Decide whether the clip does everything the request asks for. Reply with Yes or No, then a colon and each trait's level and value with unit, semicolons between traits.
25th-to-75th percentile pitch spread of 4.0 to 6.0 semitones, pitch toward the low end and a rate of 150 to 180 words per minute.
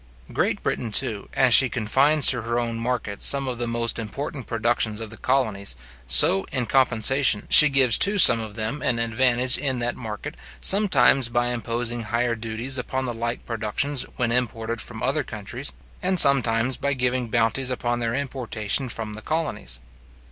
No: average, 2.7 semitones; low, 120 Hz; average, 170 wpm